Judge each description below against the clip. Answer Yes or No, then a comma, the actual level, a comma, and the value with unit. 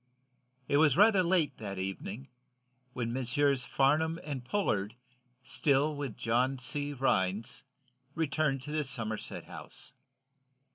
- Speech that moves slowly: Yes, slow, 115 wpm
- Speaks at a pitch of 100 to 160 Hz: Yes, low, 135 Hz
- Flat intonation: No, average, 4.4 semitones